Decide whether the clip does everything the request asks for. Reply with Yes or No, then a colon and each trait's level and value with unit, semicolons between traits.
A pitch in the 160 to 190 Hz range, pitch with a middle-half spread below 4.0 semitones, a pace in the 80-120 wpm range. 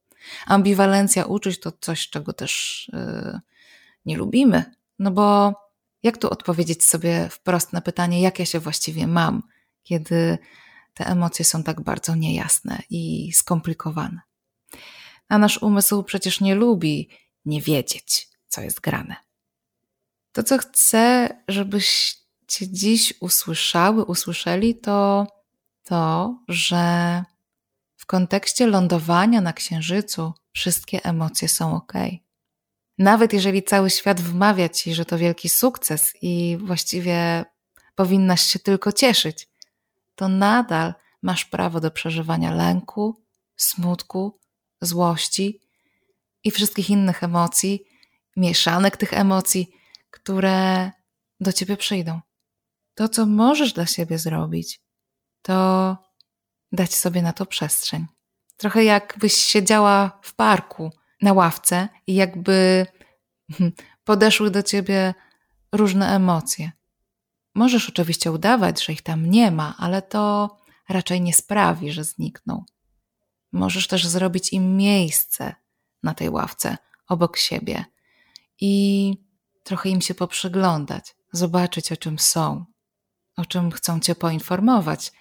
Yes: medium, 185 Hz; average, 3.0 semitones; average, 115 wpm